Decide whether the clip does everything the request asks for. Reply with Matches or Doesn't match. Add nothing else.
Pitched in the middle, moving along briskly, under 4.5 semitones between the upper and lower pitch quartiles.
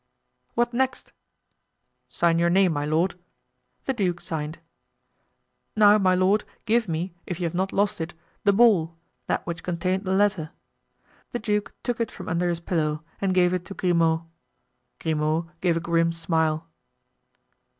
Doesn't match